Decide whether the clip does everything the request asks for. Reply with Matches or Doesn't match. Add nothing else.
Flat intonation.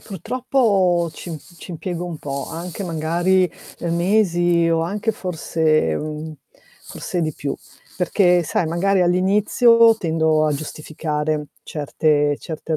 Doesn't match